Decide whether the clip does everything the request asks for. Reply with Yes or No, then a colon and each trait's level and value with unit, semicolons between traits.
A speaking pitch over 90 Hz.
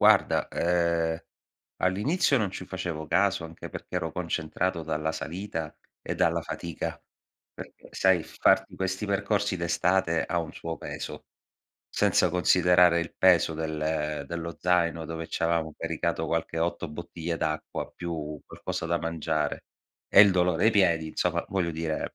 No: very low, 85 Hz